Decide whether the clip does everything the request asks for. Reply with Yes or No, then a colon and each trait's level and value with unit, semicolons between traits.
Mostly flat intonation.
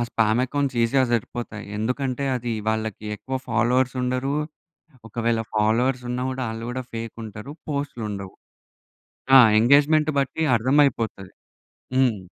No: average, 3.1 semitones